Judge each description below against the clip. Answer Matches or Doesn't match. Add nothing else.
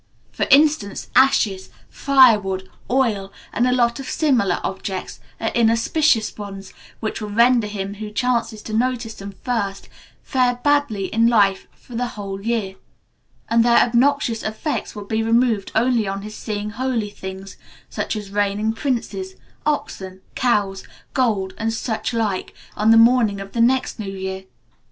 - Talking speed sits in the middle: Matches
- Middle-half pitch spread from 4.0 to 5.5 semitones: Doesn't match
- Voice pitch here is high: Matches